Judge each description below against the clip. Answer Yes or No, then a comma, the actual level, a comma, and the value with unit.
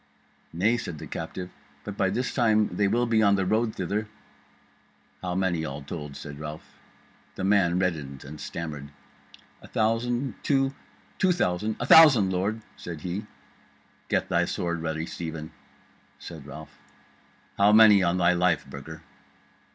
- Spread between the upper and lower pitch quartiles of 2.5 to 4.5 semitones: No, average, 5.0 semitones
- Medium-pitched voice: No, very low, 95 Hz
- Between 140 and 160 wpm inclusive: Yes, average, 150 wpm